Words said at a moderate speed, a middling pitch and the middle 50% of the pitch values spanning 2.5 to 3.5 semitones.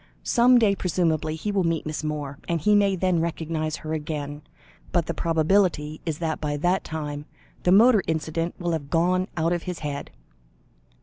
Yes: average, 180 wpm; medium, 165 Hz; average, 2.8 semitones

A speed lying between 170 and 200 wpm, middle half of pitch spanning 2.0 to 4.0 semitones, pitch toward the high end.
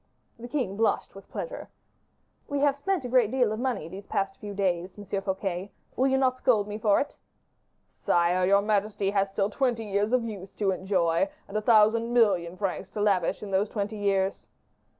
Yes: average, 190 wpm; average, 3.2 semitones; high, 205 Hz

